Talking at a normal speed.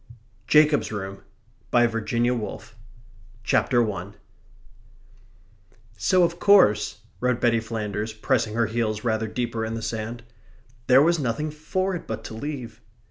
No: slow, 130 wpm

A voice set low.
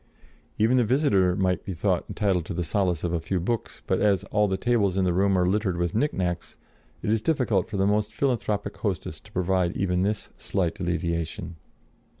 Yes: very low, 95 Hz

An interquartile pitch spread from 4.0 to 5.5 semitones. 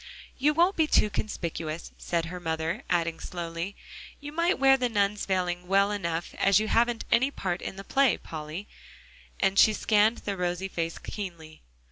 Yes: average, 4.5 semitones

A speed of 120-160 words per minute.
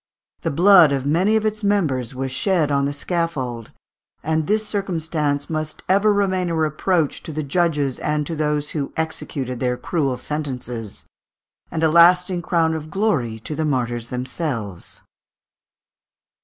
Yes: average, 150 wpm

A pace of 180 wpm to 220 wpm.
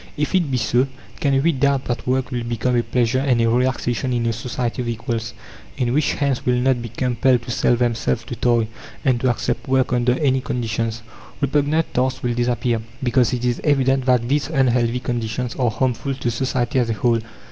Yes: average, 200 wpm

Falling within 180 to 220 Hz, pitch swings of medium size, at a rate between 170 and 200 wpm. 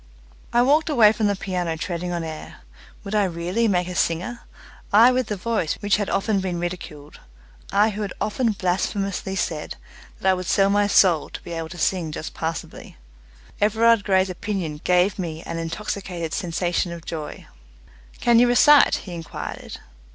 Yes: high, 190 Hz; average, 3.7 semitones; average, 175 wpm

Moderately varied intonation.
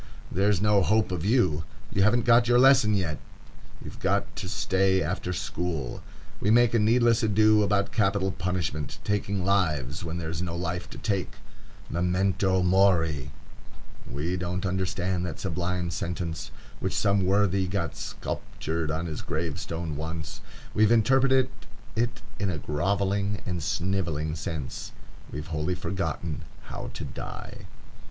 Yes: average, 3.6 semitones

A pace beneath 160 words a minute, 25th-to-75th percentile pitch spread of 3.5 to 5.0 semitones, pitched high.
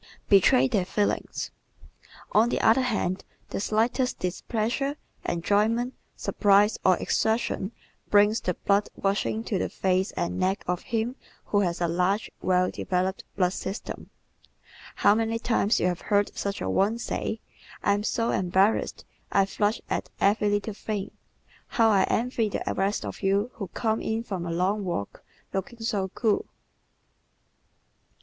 No: average, 150 wpm; average, 2.8 semitones; high, 205 Hz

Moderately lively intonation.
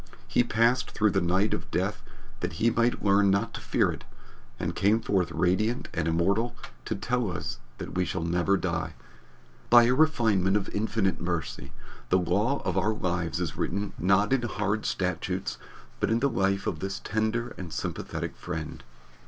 Yes: average, 3.8 semitones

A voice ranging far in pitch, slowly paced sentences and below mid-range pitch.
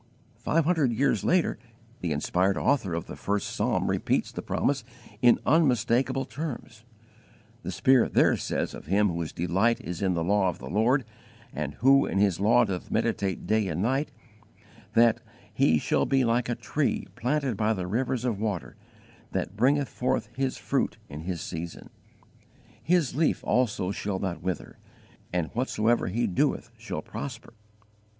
No: wide, 5.9 semitones; average, 160 wpm; low, 110 Hz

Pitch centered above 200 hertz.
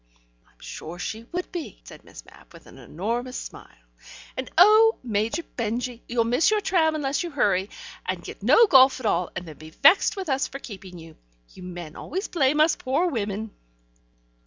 Yes: very high, 250 Hz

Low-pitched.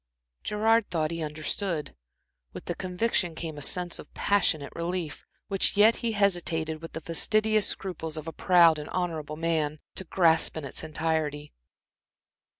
No: medium, 165 Hz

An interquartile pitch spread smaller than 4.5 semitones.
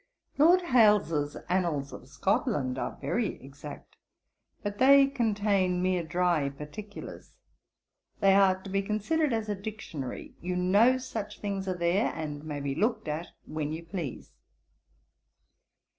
No: average, 5.3 semitones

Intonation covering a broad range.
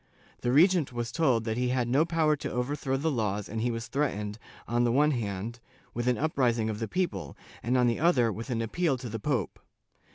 No: average, 4.1 semitones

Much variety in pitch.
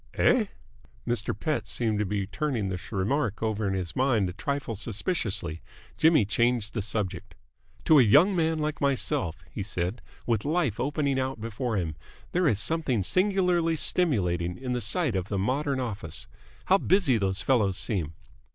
Yes: wide, 7.0 semitones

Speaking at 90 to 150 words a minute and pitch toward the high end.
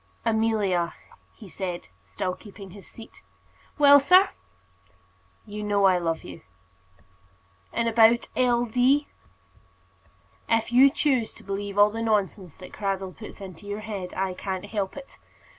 Yes: average, 140 wpm; high, 205 Hz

